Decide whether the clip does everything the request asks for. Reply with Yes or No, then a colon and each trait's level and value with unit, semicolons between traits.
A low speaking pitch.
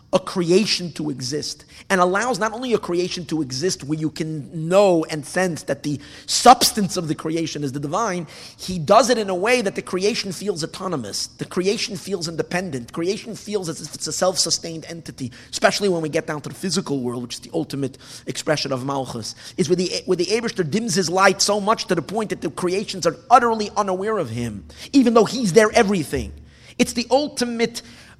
No: medium, 180 Hz